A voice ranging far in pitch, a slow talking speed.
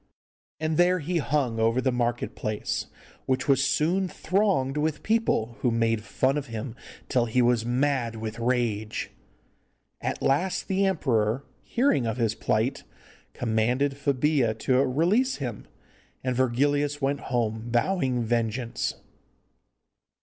No: average, 4.1 semitones; slow, 130 wpm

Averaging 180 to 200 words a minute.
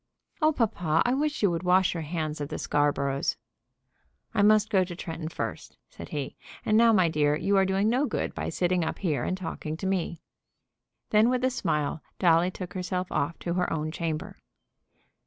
Yes: average, 195 wpm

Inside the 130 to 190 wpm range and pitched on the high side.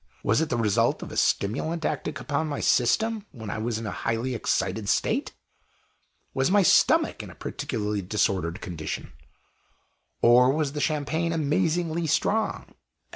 No: average, 150 wpm; low, 130 Hz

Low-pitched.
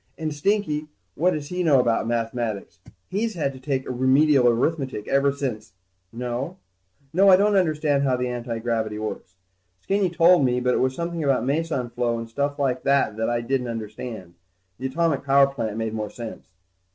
Yes: low, 130 Hz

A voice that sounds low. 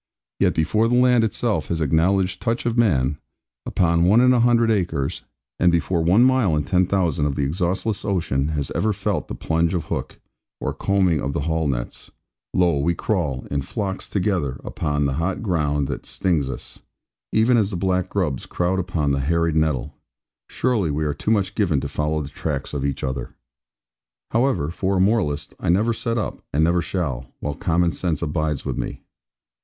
Yes: very low, 85 Hz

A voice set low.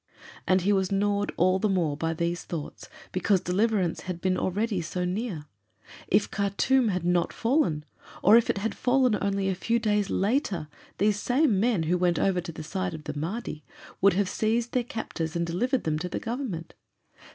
No: high, 190 Hz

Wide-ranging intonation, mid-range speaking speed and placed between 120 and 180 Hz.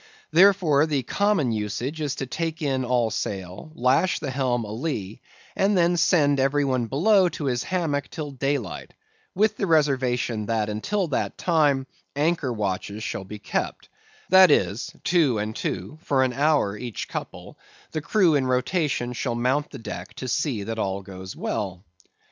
Yes: wide, 5.8 semitones; average, 165 wpm; low, 135 Hz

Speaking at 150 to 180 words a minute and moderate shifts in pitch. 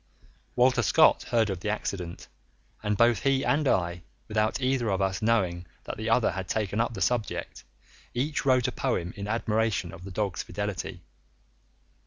Yes: average, 170 wpm; average, 3.8 semitones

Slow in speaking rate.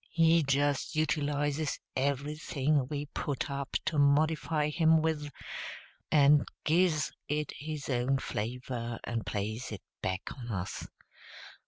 Yes: slow, 120 wpm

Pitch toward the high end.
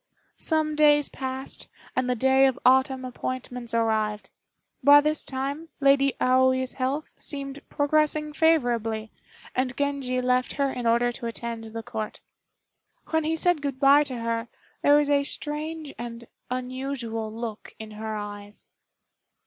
Yes: very high, 260 Hz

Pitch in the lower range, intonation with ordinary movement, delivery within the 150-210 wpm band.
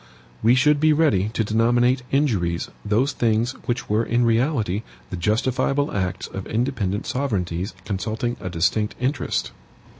No: low, 115 Hz; average, 4.2 semitones; average, 140 wpm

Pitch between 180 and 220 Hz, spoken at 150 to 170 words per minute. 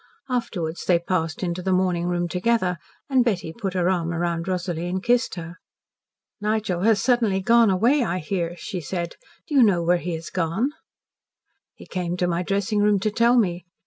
No: medium, 185 Hz; average, 185 wpm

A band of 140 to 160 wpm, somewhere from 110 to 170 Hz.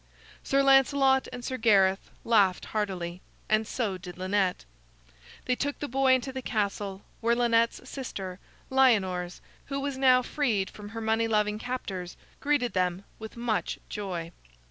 No: average, 145 wpm; high, 220 Hz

